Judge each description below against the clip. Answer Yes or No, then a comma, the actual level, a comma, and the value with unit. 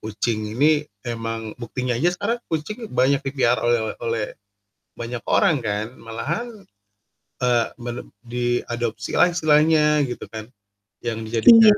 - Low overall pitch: Yes, low, 120 Hz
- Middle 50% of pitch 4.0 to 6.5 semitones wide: Yes, average, 4.8 semitones